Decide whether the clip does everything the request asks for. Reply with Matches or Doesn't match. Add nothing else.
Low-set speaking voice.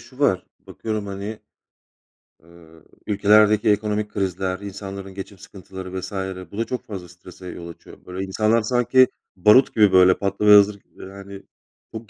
Matches